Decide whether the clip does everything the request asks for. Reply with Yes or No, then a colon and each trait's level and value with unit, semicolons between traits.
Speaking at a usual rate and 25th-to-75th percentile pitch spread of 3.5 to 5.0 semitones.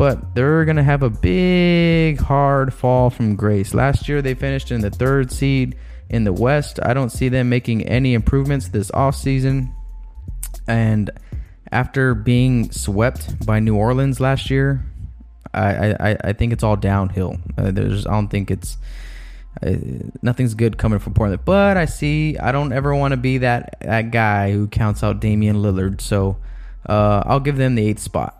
Yes: average, 175 wpm; average, 4.6 semitones